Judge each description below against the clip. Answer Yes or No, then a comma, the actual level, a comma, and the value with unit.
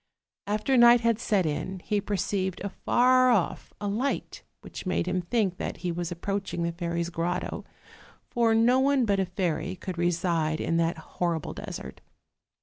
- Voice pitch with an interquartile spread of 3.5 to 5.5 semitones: Yes, average, 4.5 semitones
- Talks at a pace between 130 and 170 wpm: Yes, average, 165 wpm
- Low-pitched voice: No, medium, 185 Hz